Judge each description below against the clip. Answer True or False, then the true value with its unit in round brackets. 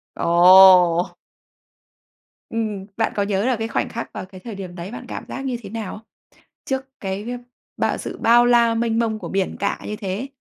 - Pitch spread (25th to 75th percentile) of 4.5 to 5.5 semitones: False (3.5 semitones)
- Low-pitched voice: False (215 Hz)